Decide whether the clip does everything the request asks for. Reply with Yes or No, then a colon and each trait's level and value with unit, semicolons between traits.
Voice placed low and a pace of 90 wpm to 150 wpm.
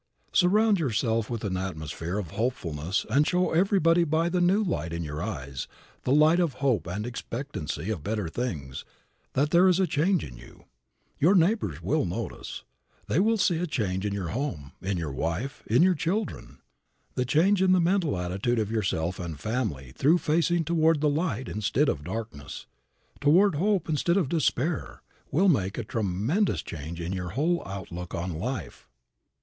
No: low, 125 Hz; average, 175 wpm